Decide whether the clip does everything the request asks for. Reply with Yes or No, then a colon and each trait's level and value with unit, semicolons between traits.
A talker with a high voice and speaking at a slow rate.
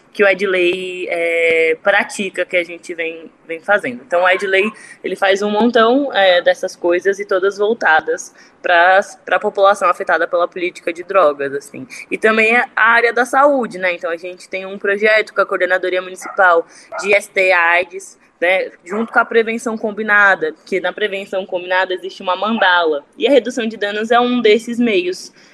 No: high, 195 Hz; average, 175 wpm